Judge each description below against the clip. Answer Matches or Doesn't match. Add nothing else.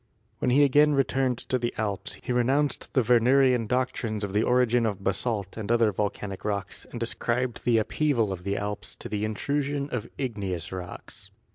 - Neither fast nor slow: Matches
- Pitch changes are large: Doesn't match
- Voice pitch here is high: Doesn't match